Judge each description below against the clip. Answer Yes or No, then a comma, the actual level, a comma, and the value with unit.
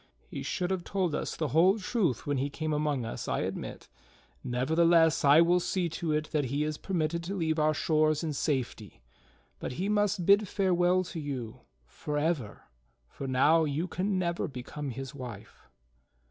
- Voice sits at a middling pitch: Yes, medium, 155 Hz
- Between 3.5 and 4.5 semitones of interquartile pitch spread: Yes, average, 3.9 semitones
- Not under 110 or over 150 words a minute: No, average, 175 wpm